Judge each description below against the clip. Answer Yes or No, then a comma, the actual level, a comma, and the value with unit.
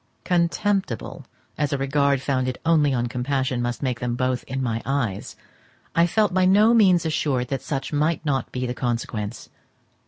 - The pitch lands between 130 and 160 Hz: Yes, low, 135 Hz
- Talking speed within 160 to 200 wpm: Yes, average, 165 wpm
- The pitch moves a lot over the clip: No, average, 4.8 semitones